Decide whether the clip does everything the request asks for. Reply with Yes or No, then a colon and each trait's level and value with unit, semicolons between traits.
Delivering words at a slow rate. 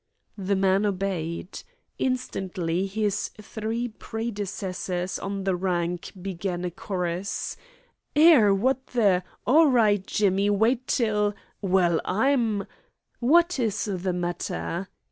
Yes: slow, 120 wpm